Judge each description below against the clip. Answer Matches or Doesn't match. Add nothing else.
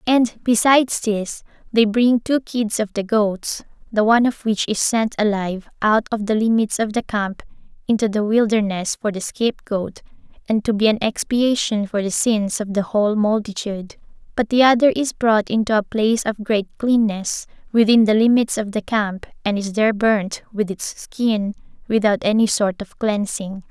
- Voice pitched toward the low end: Doesn't match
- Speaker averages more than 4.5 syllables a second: Matches